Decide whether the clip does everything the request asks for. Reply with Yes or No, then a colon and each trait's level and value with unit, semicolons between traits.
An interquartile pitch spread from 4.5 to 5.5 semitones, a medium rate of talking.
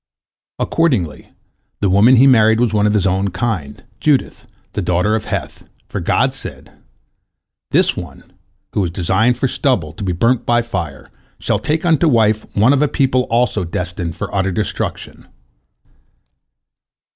Yes: average, 5.2 semitones; average, 150 wpm